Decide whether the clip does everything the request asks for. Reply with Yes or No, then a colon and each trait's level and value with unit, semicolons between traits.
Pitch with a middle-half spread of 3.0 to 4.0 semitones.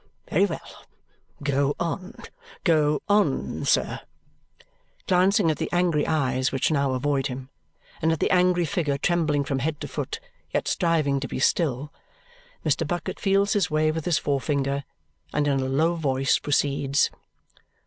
Yes: average, 3.5 semitones